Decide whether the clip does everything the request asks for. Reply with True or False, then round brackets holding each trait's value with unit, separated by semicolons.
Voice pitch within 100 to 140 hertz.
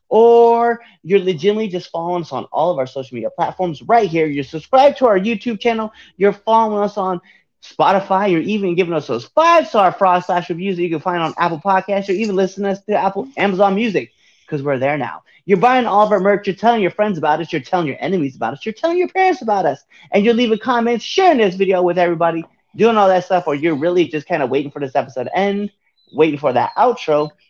False (190 Hz)